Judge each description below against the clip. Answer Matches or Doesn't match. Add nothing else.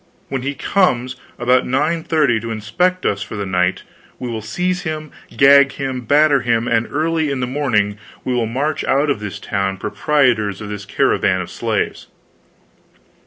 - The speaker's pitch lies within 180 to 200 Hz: Doesn't match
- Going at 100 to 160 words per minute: Doesn't match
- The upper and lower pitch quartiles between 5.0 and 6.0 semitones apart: Matches